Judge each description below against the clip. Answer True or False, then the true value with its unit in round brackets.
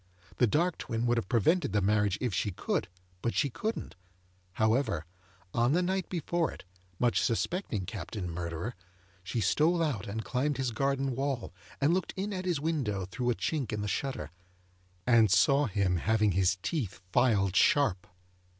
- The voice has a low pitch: True (120 Hz)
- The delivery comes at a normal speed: True (170 wpm)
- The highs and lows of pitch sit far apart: True (6.1 semitones)